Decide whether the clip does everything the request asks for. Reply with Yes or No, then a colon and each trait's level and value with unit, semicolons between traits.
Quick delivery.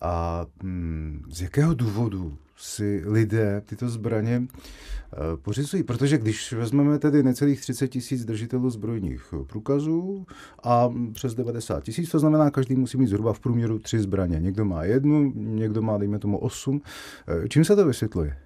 No: average, 145 wpm